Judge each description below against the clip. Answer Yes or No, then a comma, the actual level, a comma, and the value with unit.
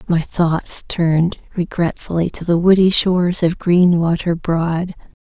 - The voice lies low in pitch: No, medium, 170 Hz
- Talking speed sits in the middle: No, slow, 125 wpm